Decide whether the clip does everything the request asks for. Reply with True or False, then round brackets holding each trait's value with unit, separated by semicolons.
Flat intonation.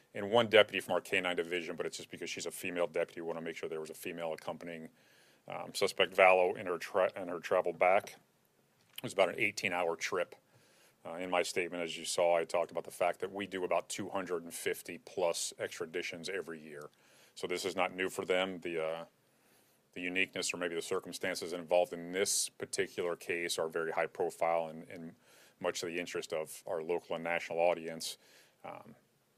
True (2.0 semitones)